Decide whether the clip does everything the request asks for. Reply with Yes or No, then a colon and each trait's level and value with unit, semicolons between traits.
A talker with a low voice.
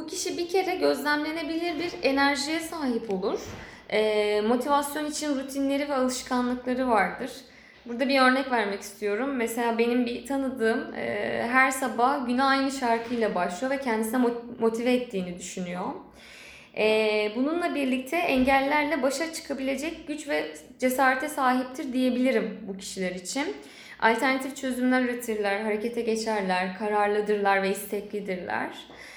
No: very high, 250 Hz